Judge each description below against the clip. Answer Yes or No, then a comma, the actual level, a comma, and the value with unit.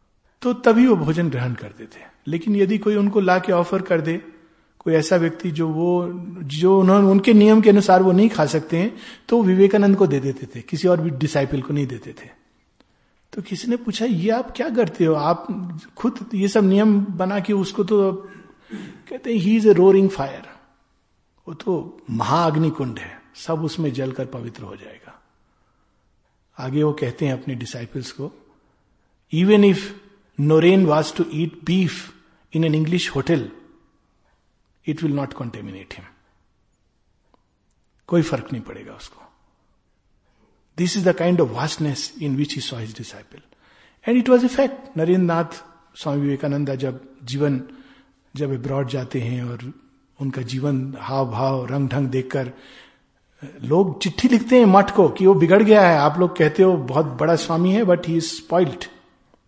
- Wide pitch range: Yes, wide, 6.0 semitones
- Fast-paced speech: No, average, 165 wpm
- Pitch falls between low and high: Yes, medium, 165 Hz